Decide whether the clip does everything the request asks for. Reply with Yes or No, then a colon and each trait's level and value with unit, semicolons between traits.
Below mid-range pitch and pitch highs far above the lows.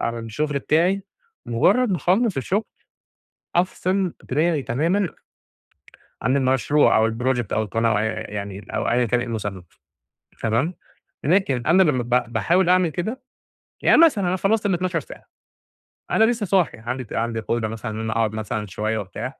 Yes: low, 130 Hz; wide, 8.5 semitones